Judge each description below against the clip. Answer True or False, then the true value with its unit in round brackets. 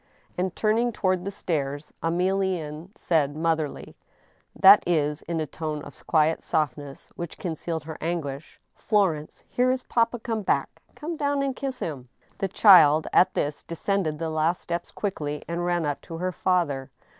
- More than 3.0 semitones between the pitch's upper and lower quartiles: True (4.2 semitones)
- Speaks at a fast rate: False (165 wpm)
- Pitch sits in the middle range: True (170 Hz)